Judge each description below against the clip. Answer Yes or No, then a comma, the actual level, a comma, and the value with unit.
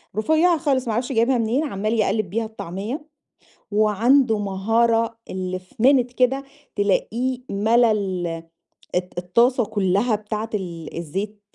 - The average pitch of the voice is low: No, high, 220 Hz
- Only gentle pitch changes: No, average, 3.7 semitones